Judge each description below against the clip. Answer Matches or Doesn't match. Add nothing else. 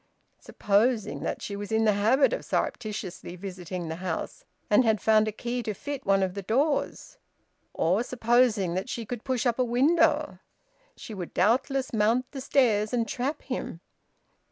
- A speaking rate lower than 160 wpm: Doesn't match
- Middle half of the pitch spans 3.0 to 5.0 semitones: Matches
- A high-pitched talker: Matches